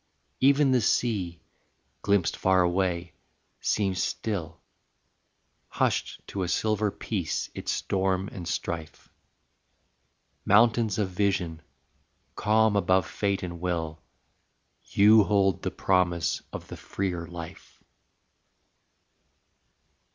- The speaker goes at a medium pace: No, slow, 100 wpm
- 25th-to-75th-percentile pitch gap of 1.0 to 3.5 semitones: Yes, average, 3.1 semitones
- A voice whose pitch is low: Yes, very low, 95 Hz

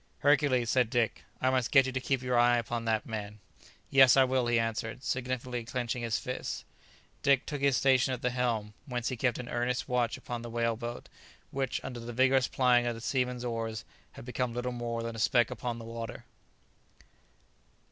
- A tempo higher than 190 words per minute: Yes, average, 200 wpm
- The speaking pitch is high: No, low, 120 Hz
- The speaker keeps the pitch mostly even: Yes, narrow, 1.6 semitones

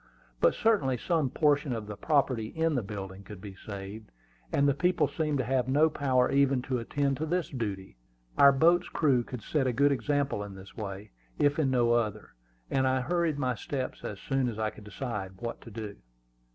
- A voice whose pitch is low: Yes, low, 130 Hz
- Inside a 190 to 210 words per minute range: Yes, fast, 205 wpm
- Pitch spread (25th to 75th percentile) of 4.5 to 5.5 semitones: Yes, average, 5.0 semitones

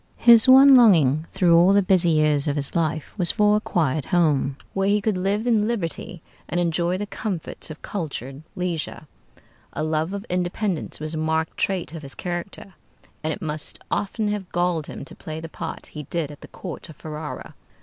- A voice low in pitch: No, medium, 170 Hz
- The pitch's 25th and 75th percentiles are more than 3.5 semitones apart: Yes, average, 4.0 semitones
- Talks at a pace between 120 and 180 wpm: No, average, 195 wpm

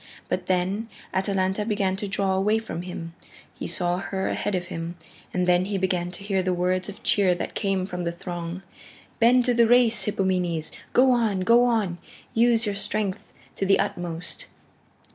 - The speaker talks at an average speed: Yes, average, 180 wpm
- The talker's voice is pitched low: No, high, 190 Hz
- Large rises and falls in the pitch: No, average, 2.8 semitones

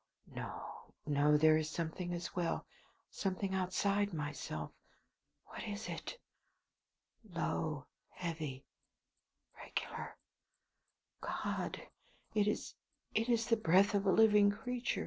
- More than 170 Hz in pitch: Yes, medium, 185 Hz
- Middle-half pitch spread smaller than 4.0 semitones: No, average, 4.7 semitones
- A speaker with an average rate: No, slow, 110 wpm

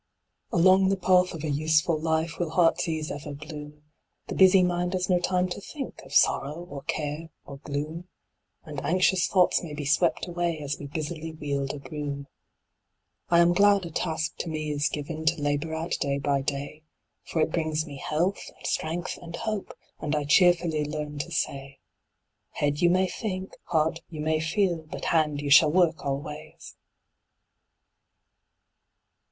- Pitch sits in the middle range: Yes, medium, 160 Hz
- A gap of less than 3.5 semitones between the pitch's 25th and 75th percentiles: Yes, average, 2.9 semitones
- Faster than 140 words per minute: Yes, average, 170 wpm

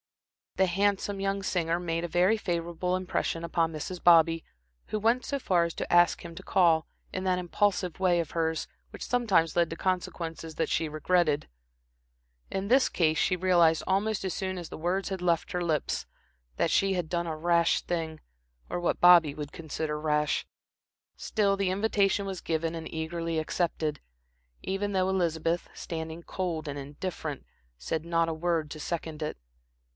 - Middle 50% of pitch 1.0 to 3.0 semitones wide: Yes, narrow, 2.6 semitones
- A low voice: No, medium, 170 Hz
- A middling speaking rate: Yes, average, 170 wpm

